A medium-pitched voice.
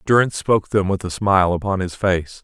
No: very low, 95 Hz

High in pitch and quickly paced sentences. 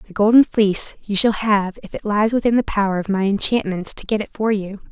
Yes: high, 205 Hz; fast, 245 wpm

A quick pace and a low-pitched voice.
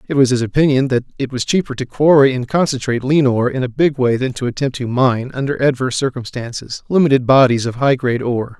Yes: fast, 225 wpm; low, 130 Hz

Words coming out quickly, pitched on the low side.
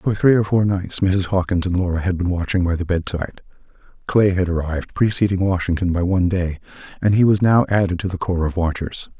Yes: fast, 215 wpm; very low, 90 Hz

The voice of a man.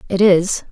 No: female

